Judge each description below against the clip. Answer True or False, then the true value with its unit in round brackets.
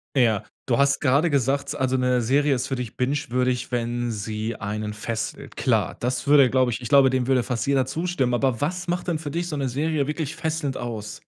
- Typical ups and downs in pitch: True (3.0 semitones)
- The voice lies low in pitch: True (130 Hz)